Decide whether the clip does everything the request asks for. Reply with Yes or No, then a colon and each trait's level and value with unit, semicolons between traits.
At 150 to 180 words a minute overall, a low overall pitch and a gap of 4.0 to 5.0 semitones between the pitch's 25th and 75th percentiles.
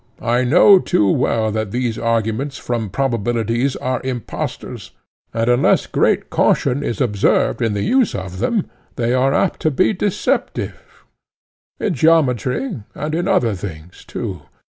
No: average, 140 wpm; low, 125 Hz; average, 4.7 semitones